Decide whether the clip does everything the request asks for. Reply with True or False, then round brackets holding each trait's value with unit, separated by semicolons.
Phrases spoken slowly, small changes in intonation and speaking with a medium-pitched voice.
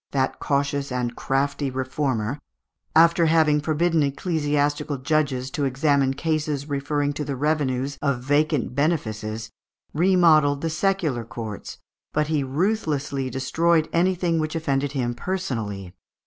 False (120 wpm; 3.0 semitones; 145 Hz)